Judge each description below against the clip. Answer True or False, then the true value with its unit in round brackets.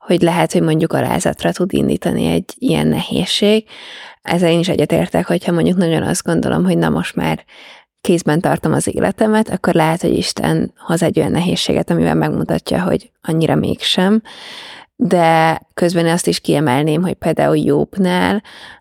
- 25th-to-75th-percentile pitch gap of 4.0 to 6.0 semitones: False (2.6 semitones)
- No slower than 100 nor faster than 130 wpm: False (155 wpm)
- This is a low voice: False (170 Hz)